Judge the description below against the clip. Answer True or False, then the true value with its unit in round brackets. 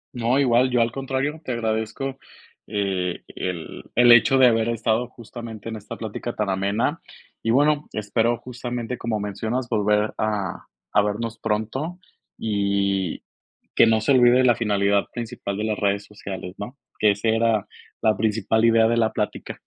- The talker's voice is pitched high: False (110 Hz)